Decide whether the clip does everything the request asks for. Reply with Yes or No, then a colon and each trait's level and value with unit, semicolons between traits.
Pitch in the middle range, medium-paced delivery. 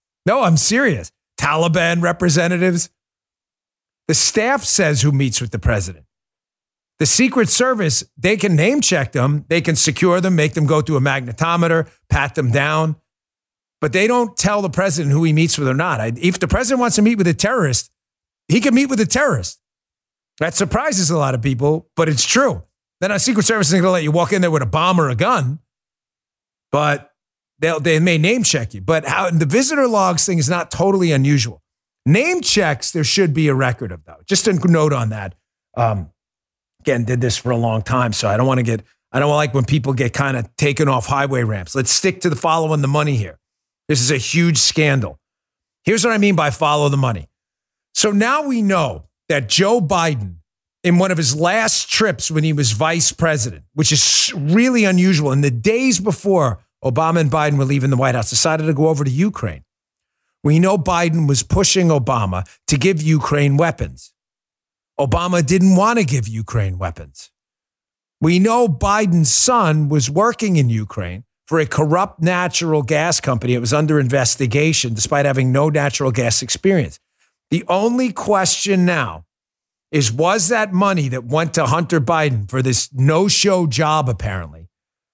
Yes: medium, 155 Hz; average, 190 wpm